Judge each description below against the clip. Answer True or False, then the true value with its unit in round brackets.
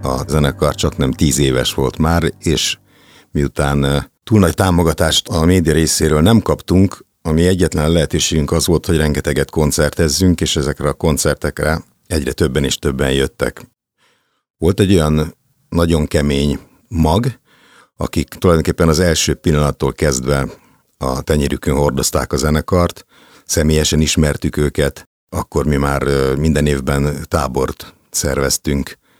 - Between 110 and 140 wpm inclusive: True (125 wpm)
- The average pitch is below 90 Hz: True (75 Hz)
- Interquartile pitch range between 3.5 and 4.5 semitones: False (2.8 semitones)